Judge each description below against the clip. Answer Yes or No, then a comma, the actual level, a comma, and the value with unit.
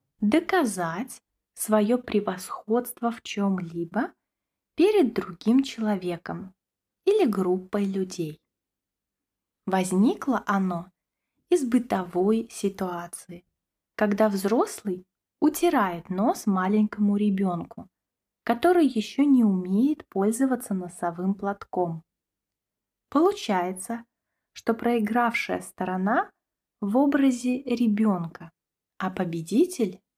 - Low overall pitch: No, high, 210 Hz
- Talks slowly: Yes, slow, 75 wpm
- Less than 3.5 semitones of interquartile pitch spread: No, average, 4.8 semitones